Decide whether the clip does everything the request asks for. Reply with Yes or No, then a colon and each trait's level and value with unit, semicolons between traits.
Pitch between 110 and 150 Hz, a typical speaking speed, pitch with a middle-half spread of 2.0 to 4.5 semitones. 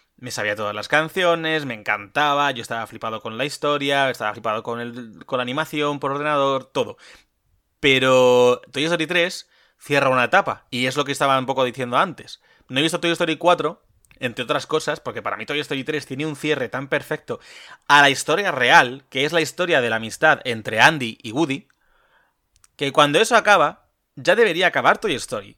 No: medium, 140 Hz; fast, 195 wpm; average, 3.9 semitones